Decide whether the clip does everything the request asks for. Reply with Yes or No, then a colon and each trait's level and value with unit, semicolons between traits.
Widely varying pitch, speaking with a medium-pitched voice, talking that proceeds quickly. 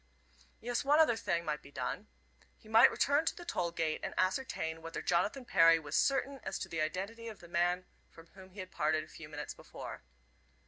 Yes: wide, 6.2 semitones; medium, 180 Hz; fast, 210 wpm